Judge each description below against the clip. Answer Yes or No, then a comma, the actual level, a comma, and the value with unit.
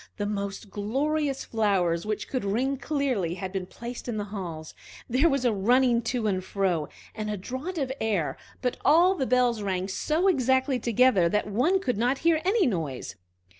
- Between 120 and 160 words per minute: No, average, 180 wpm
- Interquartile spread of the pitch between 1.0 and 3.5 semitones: No, average, 5.2 semitones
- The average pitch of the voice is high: Yes, high, 235 Hz